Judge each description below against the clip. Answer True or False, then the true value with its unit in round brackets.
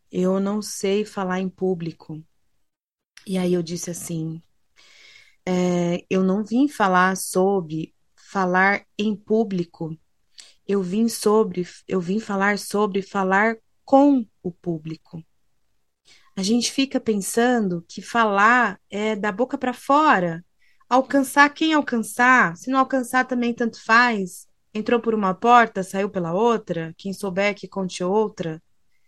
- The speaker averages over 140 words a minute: False (130 wpm)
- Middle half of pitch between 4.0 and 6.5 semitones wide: True (4.3 semitones)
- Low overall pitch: False (200 Hz)